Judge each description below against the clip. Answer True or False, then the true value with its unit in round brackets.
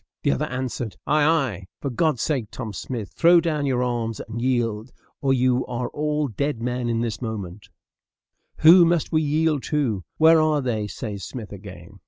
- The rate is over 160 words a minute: True (175 wpm)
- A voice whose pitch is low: True (125 Hz)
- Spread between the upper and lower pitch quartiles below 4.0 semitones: False (5.1 semitones)